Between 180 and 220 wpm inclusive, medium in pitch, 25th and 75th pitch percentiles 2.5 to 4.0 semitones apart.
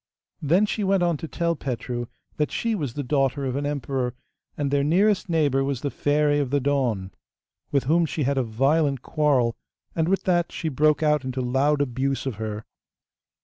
Yes: average, 190 wpm; medium, 145 Hz; average, 3.1 semitones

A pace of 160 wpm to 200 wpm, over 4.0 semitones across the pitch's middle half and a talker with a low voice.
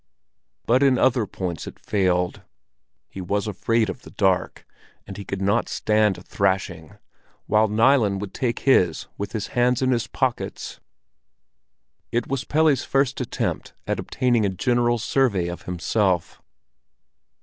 No: average, 145 wpm; average, 4.6 semitones; low, 110 Hz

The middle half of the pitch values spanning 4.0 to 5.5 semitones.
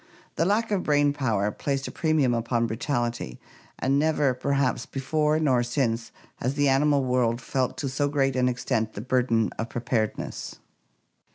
No: average, 3.2 semitones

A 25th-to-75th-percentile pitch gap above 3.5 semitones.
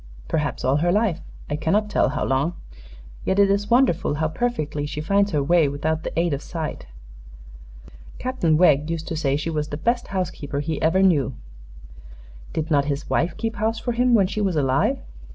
Yes: average, 5.3 semitones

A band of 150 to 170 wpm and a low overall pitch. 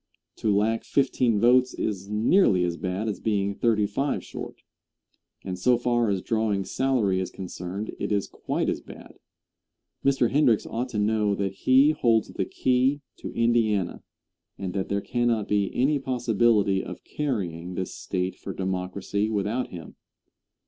Yes: average, 155 wpm; low, 105 Hz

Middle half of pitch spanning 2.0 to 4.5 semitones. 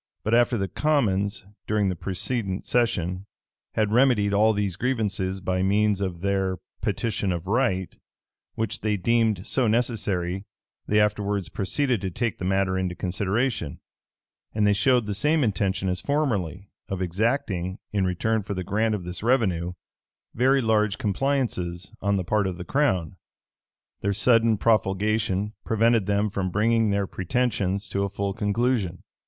Yes: average, 3.2 semitones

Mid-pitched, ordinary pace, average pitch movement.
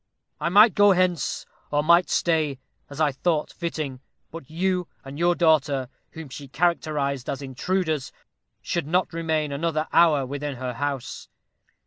Yes: medium, 155 Hz; average, 145 wpm; average, 3.5 semitones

